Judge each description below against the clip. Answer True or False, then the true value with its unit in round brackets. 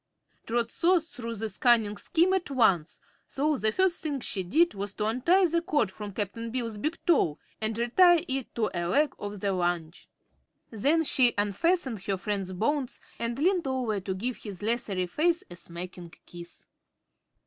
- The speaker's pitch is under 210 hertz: False (230 Hz)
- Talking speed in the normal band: True (170 wpm)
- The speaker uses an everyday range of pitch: False (7.1 semitones)